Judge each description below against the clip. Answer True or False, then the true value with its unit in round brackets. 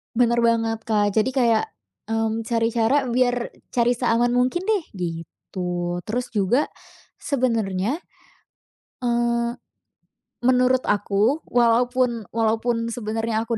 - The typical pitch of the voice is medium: False (230 Hz)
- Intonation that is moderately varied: False (2.2 semitones)